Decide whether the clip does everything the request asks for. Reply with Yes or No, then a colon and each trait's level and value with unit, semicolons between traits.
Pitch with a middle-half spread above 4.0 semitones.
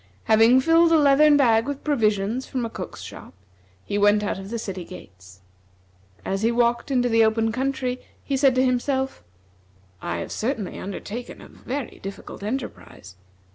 Yes: average, 4.4 semitones